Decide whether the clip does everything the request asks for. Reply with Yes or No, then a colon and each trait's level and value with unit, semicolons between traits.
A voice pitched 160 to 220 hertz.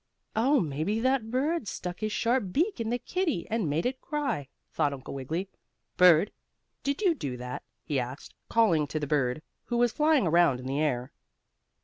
Yes: high, 190 Hz